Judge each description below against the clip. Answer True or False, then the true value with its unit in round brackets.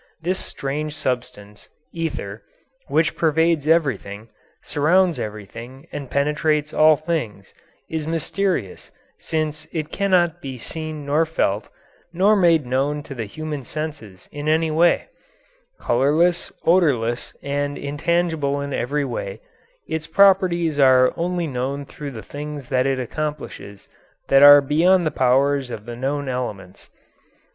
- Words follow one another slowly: True (130 wpm)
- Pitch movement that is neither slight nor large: True (4.0 semitones)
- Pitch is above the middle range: False (145 Hz)